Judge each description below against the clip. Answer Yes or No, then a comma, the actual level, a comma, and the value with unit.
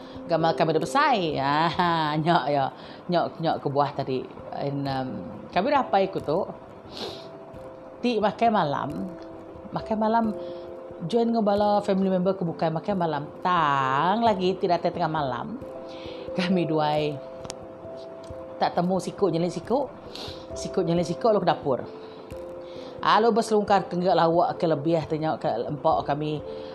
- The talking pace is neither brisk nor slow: Yes, average, 140 wpm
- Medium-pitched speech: Yes, medium, 170 Hz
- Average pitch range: Yes, average, 4.8 semitones